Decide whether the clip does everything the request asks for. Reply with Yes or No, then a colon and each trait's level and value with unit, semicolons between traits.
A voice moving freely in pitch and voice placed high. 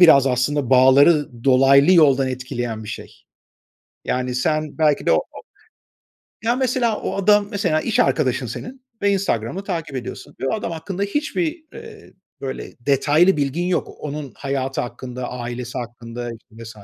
No: wide, 6.8 semitones; medium, 140 Hz